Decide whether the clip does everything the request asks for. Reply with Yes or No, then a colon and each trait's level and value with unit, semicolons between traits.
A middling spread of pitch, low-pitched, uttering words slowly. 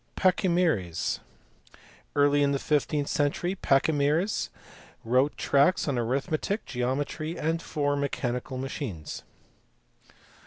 No: average, 3.4 semitones; medium, 145 Hz; slow, 90 wpm